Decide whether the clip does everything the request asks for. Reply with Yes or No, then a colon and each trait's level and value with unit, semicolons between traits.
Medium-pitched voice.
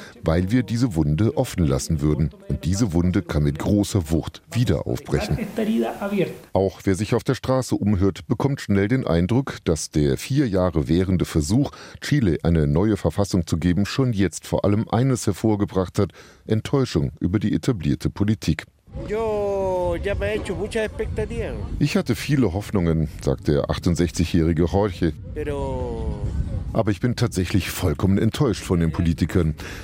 No: low, 100 Hz